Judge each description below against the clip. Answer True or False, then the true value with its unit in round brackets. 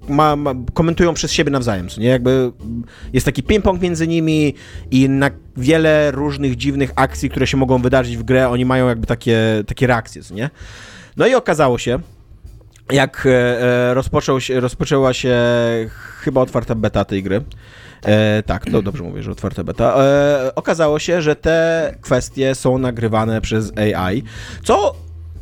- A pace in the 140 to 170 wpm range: True (160 wpm)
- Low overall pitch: True (130 Hz)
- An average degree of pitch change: True (4.1 semitones)